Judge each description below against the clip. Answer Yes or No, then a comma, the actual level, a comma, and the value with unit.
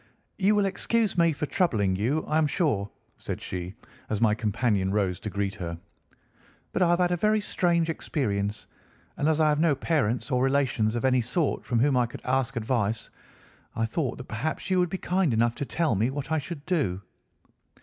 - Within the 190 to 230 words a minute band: Yes, average, 200 wpm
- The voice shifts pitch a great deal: Yes, wide, 7.1 semitones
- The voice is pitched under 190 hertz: Yes, low, 135 Hz